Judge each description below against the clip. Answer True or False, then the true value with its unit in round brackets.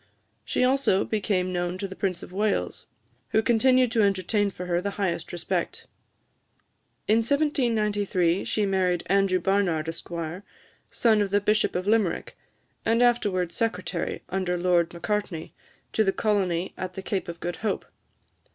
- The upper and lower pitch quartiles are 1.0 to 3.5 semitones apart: True (3.2 semitones)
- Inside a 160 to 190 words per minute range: False (150 wpm)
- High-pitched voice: True (195 Hz)